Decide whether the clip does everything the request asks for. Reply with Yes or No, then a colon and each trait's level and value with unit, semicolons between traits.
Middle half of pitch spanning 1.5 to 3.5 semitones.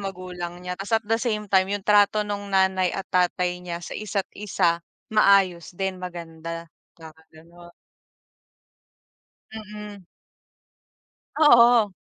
Yes: average, 3.0 semitones